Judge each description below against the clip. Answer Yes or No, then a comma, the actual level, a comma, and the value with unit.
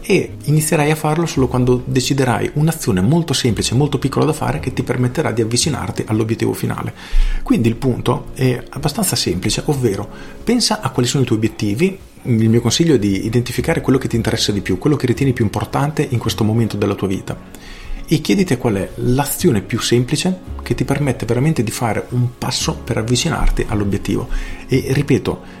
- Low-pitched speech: Yes, low, 125 Hz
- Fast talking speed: Yes, fast, 185 wpm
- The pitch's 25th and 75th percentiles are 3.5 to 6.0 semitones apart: Yes, average, 3.9 semitones